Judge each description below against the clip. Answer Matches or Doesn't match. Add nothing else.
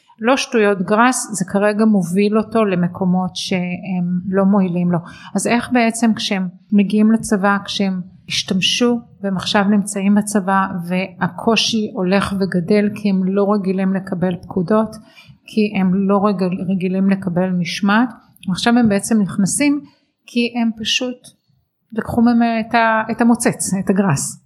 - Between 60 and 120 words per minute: Doesn't match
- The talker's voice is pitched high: Matches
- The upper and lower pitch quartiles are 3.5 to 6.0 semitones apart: Doesn't match